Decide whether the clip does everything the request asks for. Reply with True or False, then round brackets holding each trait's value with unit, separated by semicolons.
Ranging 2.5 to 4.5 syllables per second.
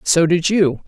True (3.9 syllables/s)